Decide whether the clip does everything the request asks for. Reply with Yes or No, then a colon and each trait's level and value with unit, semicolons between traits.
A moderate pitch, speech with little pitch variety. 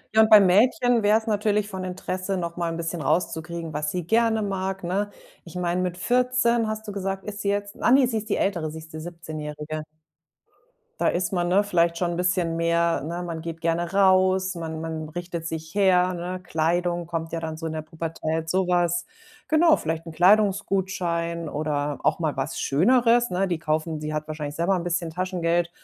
No: medium, 175 Hz; average, 3.1 semitones